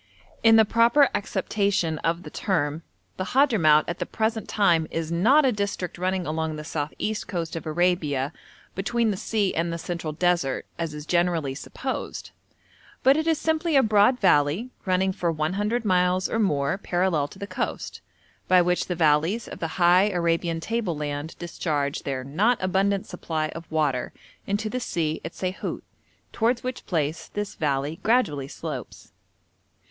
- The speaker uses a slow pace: No, average, 165 wpm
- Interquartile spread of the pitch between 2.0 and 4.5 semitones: No, average, 4.9 semitones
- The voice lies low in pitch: No, medium, 180 Hz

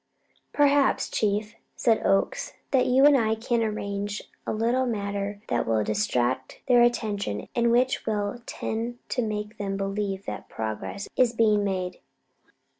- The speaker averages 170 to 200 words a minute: No, average, 145 wpm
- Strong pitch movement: No, average, 3.1 semitones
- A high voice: Yes, high, 215 Hz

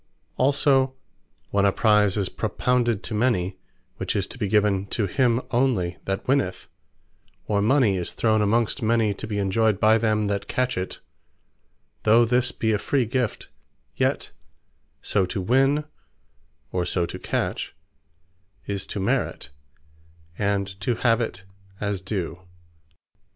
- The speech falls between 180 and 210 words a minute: No, average, 140 wpm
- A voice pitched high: No, low, 105 Hz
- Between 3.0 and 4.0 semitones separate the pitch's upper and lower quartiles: Yes, average, 3.5 semitones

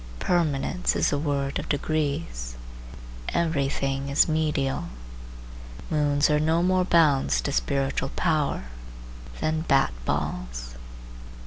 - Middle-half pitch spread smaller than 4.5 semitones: Yes, average, 2.7 semitones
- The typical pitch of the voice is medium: Yes, medium, 145 Hz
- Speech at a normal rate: No, slow, 110 wpm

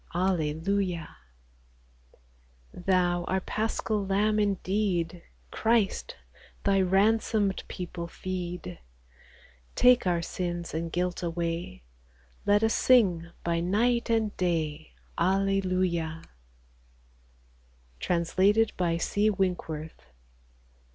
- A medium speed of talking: No, slow, 85 wpm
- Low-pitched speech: No, medium, 185 Hz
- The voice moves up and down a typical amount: Yes, average, 3.0 semitones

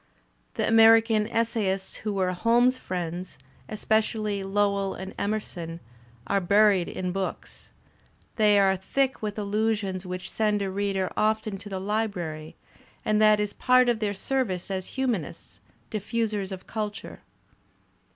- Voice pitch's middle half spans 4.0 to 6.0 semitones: No, narrow, 2.4 semitones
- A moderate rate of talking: No, slow, 130 wpm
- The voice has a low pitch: No, high, 205 Hz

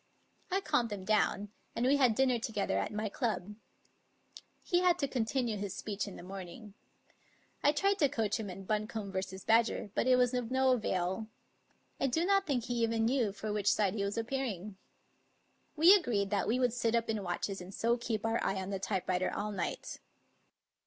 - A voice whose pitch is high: Yes, high, 225 Hz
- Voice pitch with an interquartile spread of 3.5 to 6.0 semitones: Yes, average, 3.9 semitones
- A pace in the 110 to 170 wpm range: No, average, 195 wpm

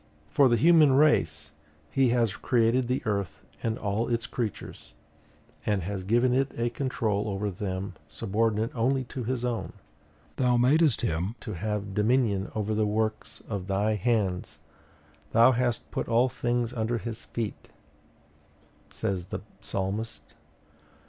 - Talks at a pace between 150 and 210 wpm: No, average, 140 wpm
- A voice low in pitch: Yes, low, 110 Hz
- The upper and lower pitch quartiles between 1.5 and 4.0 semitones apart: Yes, average, 3.3 semitones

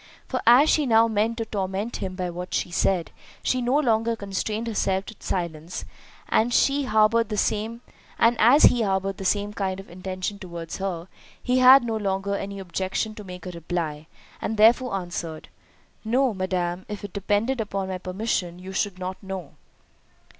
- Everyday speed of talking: Yes, average, 155 wpm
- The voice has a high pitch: Yes, high, 200 Hz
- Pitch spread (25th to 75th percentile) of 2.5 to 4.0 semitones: Yes, average, 3.5 semitones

